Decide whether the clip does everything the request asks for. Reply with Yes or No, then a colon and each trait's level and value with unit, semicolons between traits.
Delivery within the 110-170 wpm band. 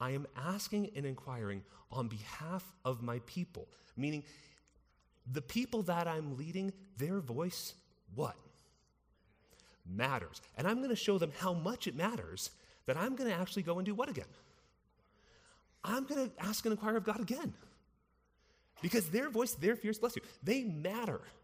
Yes: average, 160 wpm